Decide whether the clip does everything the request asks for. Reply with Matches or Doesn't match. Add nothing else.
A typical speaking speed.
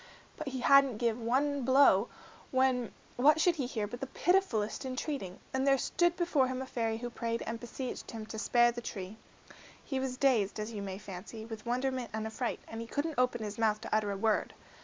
Doesn't match